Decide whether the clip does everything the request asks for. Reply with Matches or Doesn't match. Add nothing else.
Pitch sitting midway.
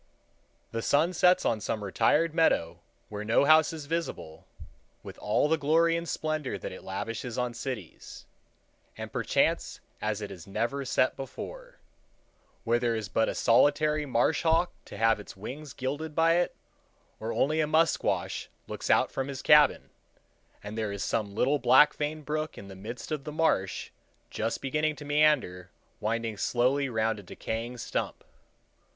Doesn't match